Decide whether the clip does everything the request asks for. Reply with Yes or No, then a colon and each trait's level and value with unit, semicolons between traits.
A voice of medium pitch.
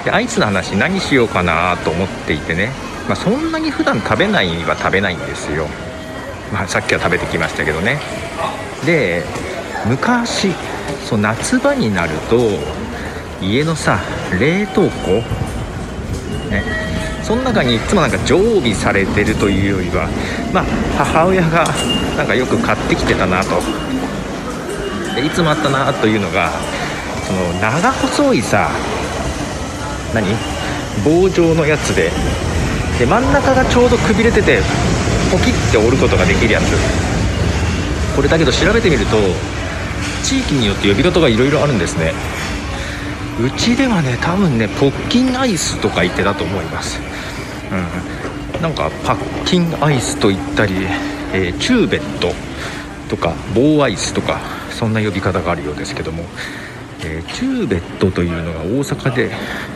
No: low, 100 Hz